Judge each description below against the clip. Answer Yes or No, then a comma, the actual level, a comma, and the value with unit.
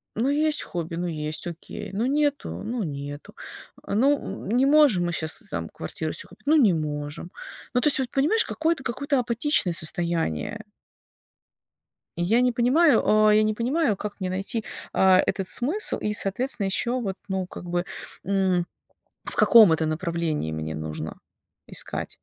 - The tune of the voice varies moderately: No, wide, 7.1 semitones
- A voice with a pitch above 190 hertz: Yes, high, 205 Hz